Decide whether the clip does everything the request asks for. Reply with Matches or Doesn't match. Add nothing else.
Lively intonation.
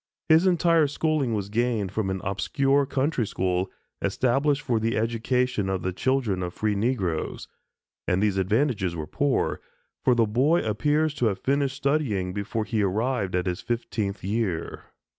Matches